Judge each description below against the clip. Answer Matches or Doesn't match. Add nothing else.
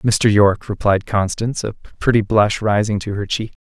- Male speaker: Matches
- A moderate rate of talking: Matches